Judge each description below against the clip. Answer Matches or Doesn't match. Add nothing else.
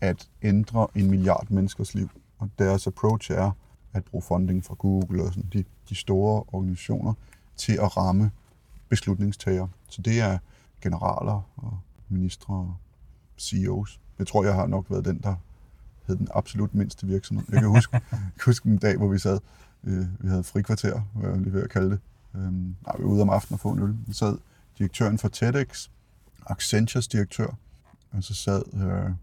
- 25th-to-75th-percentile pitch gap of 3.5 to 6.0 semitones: Doesn't match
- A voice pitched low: Matches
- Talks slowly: Doesn't match